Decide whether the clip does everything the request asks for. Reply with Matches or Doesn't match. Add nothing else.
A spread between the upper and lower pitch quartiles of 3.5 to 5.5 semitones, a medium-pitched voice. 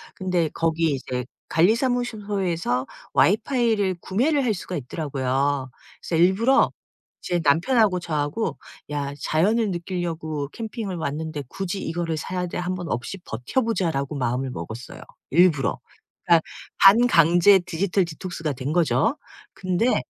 Matches